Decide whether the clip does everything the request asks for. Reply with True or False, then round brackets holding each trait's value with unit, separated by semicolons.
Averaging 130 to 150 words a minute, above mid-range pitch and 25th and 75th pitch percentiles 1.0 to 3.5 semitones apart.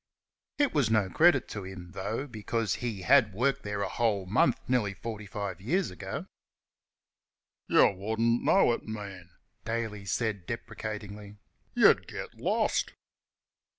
False (145 wpm; 110 Hz; 2.8 semitones)